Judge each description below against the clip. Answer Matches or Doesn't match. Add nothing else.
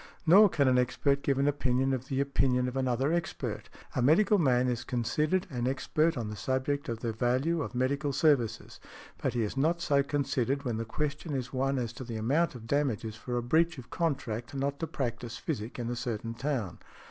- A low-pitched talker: Matches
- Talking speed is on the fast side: Matches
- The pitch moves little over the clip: Doesn't match